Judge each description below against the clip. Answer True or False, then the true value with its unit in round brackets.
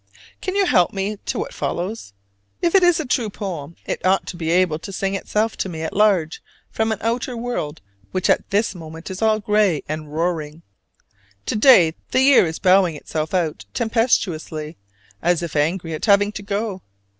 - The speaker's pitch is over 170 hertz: True (190 Hz)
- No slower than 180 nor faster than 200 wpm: True (190 wpm)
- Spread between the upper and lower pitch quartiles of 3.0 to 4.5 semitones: False (5.1 semitones)